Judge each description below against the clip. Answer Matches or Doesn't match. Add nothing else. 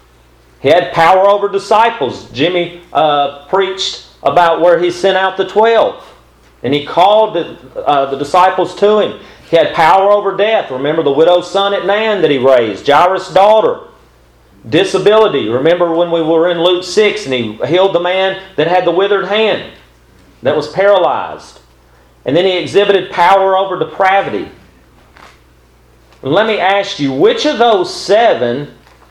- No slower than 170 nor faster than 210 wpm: Doesn't match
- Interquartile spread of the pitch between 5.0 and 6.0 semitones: Matches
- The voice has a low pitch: Doesn't match